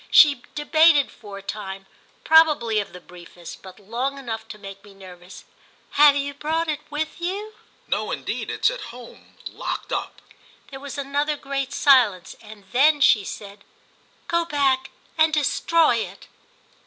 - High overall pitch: Yes, very high, 270 Hz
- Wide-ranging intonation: Yes, wide, 6.4 semitones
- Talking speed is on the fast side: No, average, 155 wpm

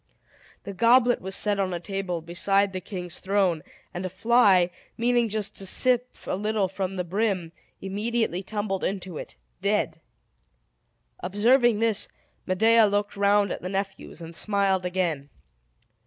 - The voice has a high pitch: Yes, high, 195 Hz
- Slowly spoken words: No, average, 145 wpm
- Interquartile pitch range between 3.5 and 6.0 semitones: No, average, 2.7 semitones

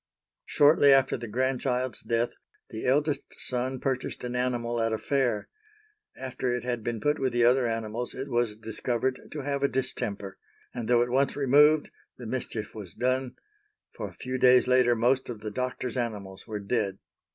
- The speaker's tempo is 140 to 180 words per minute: Yes, average, 175 wpm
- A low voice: Yes, low, 125 Hz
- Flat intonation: Yes, narrow, 2.3 semitones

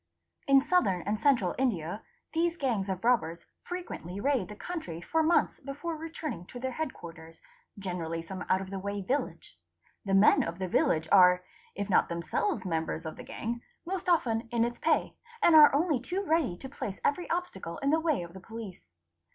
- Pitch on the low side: No, high, 225 Hz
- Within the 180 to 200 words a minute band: Yes, average, 190 wpm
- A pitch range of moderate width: No, wide, 8.6 semitones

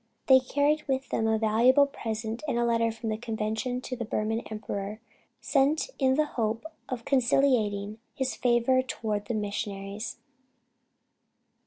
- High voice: Yes, high, 230 Hz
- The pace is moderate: Yes, average, 145 wpm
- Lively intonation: No, average, 3.3 semitones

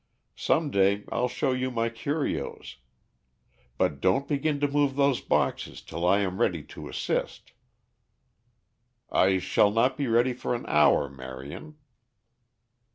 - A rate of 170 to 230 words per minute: No, slow, 135 wpm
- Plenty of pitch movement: Yes, wide, 7.1 semitones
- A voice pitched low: Yes, low, 115 Hz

